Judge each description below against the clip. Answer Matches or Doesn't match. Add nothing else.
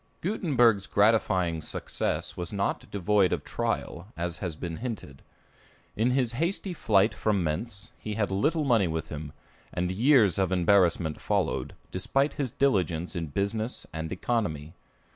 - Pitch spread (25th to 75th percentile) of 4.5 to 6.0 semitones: Matches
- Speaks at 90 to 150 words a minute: Matches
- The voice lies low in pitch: Matches